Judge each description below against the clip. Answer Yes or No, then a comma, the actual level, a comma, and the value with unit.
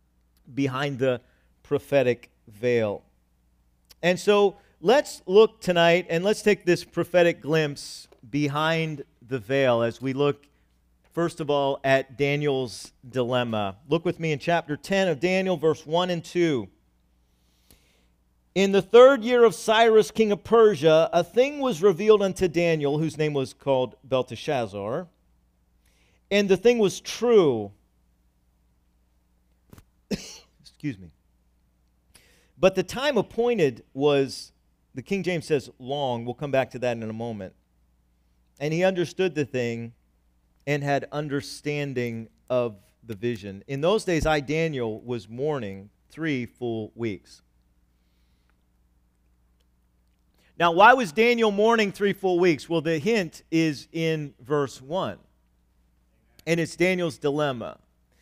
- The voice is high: No, low, 135 Hz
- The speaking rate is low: Yes, slow, 130 wpm